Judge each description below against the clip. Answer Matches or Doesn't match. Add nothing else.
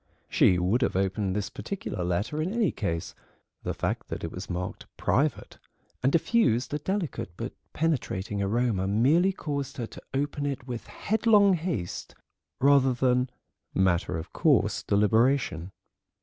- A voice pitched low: Matches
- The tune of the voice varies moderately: Doesn't match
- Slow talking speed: Doesn't match